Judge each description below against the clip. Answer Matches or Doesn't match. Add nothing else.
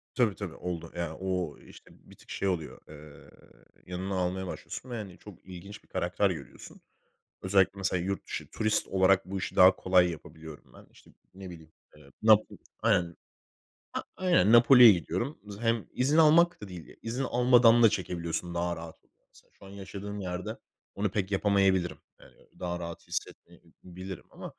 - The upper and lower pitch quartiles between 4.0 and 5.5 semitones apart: Doesn't match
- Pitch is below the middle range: Matches